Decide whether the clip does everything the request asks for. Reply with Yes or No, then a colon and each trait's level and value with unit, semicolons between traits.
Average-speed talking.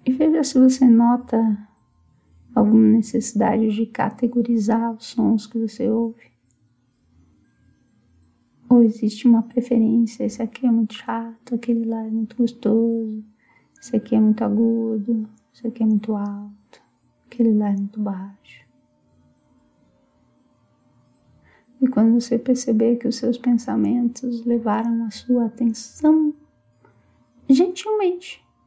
No: slow, 115 wpm